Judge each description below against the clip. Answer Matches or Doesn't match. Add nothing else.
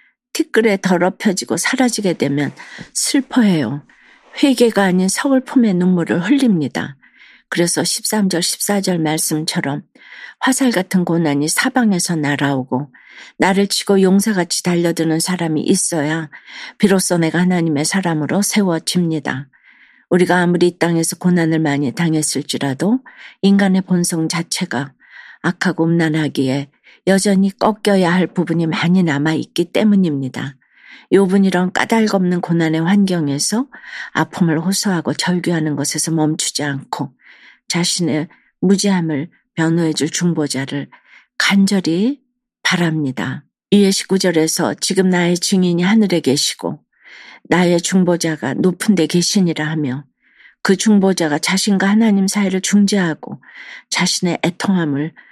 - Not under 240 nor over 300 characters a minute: Matches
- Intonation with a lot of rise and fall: Doesn't match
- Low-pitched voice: Doesn't match